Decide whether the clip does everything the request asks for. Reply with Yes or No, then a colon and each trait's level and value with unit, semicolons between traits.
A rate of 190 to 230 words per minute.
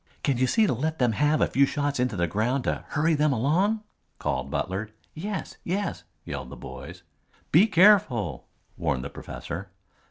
No: average, 170 wpm